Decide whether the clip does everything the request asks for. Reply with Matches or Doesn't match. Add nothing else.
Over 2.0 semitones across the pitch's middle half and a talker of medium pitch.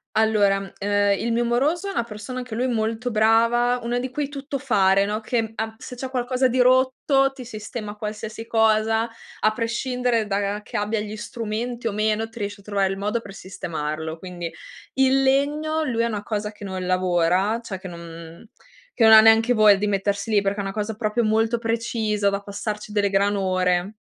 Doesn't match